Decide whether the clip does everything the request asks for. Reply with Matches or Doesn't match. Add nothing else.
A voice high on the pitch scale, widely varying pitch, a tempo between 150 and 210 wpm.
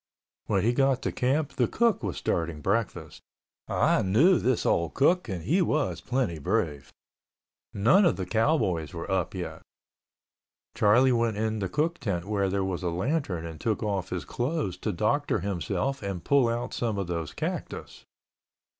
Doesn't match